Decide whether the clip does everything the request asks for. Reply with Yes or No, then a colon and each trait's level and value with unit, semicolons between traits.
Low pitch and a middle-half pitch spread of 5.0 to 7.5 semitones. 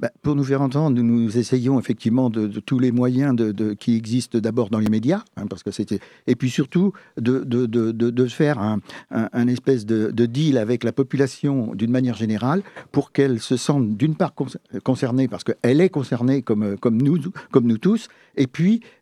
No: low, 125 Hz; average, 3.3 semitones